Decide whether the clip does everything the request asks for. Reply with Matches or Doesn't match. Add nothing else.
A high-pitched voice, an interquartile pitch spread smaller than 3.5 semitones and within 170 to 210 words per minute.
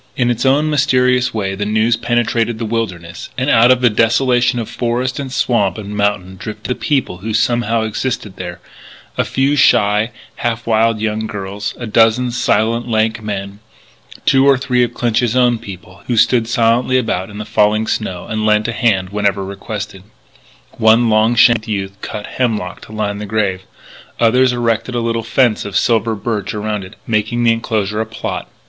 Doesn't match